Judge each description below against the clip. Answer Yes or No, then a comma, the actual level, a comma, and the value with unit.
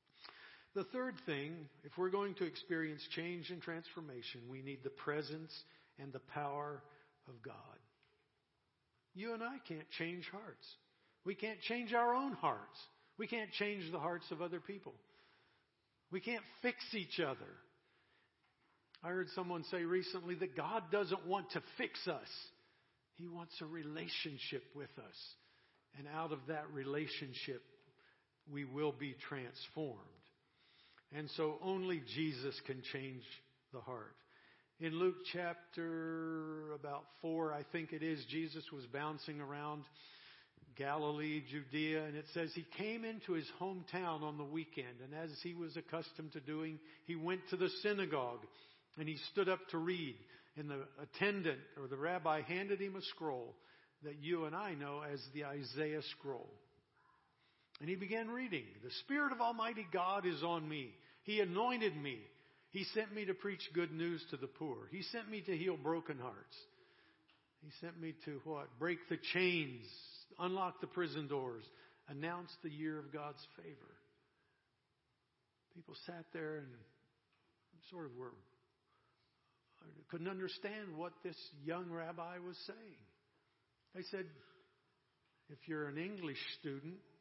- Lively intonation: No, average, 3.8 semitones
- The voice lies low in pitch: No, medium, 160 Hz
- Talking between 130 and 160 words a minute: Yes, average, 150 wpm